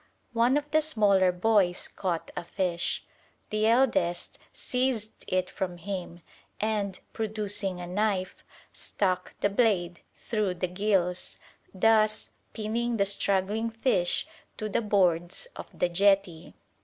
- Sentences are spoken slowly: Yes, slow, 125 wpm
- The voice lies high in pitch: Yes, high, 200 Hz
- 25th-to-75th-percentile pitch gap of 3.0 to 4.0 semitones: Yes, average, 3.3 semitones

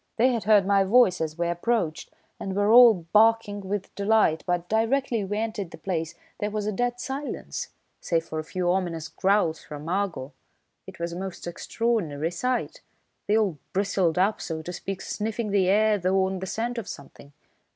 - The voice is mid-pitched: No, high, 195 Hz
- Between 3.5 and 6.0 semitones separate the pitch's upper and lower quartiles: Yes, average, 4.1 semitones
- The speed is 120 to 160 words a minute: No, average, 185 wpm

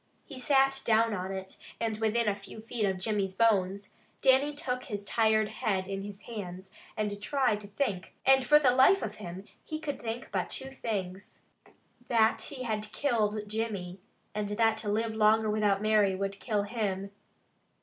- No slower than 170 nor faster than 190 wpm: Yes, average, 175 wpm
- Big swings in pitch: No, average, 2.9 semitones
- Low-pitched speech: No, high, 215 Hz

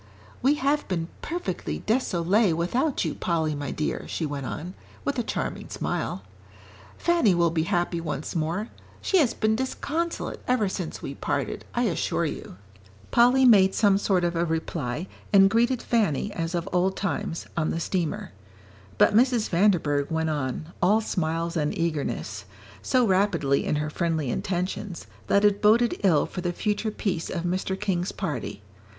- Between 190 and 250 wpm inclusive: No, average, 160 wpm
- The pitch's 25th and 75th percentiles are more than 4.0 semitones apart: Yes, average, 5.0 semitones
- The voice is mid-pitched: Yes, medium, 180 Hz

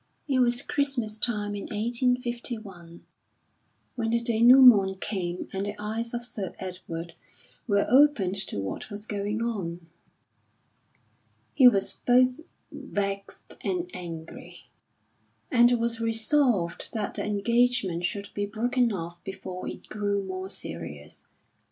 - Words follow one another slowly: Yes, slow, 120 wpm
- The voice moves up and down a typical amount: Yes, average, 4.1 semitones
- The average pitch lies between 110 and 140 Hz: No, high, 210 Hz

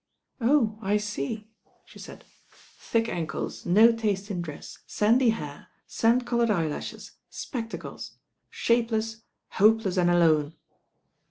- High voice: Yes, high, 215 Hz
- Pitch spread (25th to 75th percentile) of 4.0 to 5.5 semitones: Yes, average, 4.6 semitones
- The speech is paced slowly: Yes, slow, 110 wpm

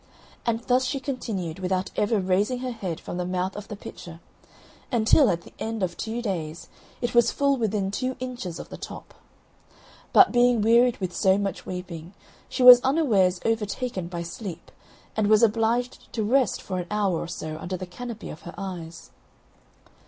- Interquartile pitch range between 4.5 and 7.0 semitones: Yes, average, 4.9 semitones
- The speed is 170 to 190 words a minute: Yes, average, 180 wpm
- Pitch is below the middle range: No, high, 210 Hz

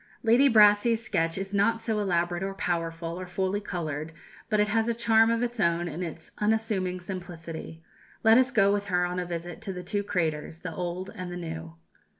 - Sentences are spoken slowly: No, average, 200 wpm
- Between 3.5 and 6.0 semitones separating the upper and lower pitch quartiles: Yes, average, 4.0 semitones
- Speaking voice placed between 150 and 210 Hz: Yes, medium, 185 Hz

